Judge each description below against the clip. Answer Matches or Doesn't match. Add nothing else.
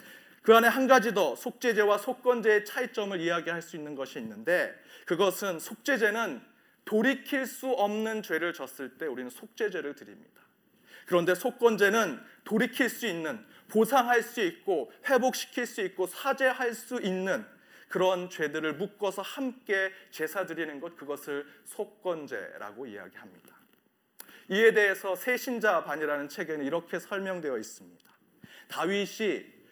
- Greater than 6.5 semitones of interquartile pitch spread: Doesn't match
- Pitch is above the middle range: Matches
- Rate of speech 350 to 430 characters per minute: Doesn't match